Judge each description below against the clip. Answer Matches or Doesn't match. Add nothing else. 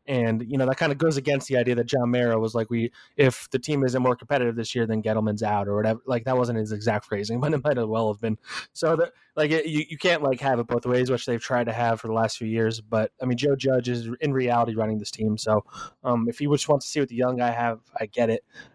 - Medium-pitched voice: Doesn't match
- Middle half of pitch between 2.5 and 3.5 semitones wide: Matches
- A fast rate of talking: Matches